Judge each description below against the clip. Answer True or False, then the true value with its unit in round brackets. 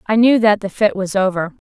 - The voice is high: True (205 Hz)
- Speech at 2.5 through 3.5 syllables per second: False (5.5 syllables/s)